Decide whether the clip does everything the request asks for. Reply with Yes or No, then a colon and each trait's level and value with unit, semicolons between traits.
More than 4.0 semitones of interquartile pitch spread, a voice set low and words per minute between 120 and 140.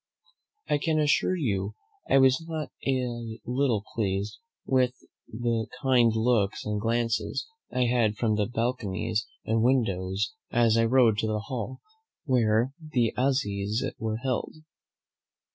No: average, 3.1 semitones; low, 115 Hz; slow, 135 wpm